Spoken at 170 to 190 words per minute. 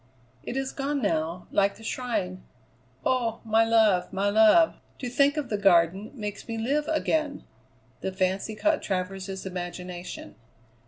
No: average, 145 wpm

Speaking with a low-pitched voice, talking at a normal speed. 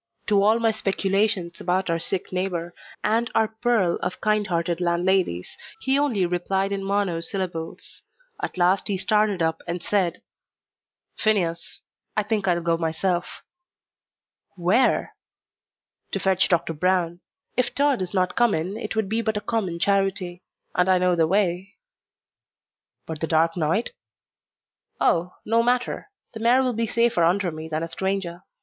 No: high, 190 Hz; average, 155 wpm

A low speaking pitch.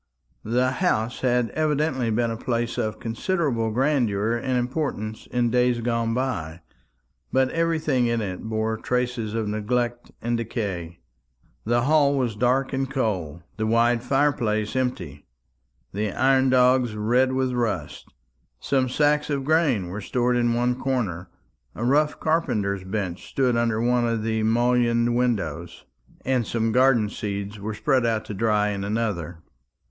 Yes: low, 120 Hz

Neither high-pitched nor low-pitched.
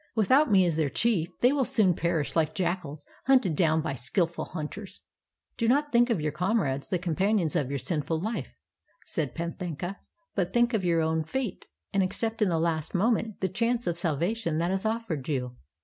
Yes: medium, 175 Hz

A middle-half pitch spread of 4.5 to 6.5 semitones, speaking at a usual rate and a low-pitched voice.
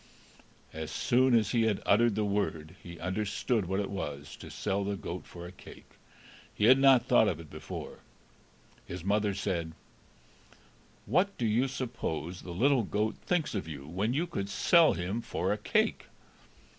Yes: average, 5.1 semitones; average, 170 wpm; low, 100 Hz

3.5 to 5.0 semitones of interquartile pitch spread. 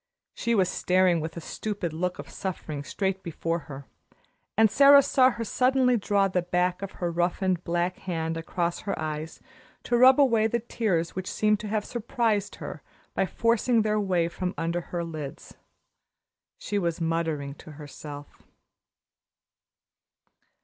Yes: average, 4.5 semitones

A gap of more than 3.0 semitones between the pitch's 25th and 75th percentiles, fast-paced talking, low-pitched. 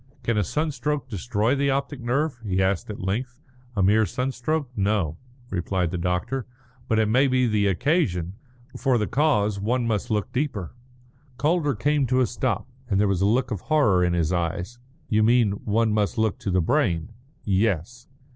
No: average, 4.9 semitones; average, 180 wpm; low, 110 Hz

